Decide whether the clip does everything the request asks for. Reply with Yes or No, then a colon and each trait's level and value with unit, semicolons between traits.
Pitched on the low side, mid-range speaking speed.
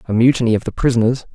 No: low, 120 Hz; fast, 225 wpm